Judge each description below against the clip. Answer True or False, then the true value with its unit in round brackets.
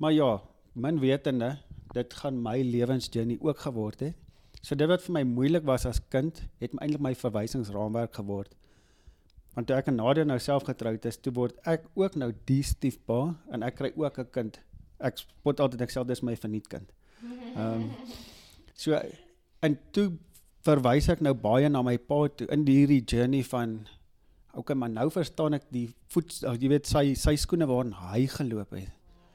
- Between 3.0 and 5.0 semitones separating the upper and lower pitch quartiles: True (4.1 semitones)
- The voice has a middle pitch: False (130 Hz)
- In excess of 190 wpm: False (180 wpm)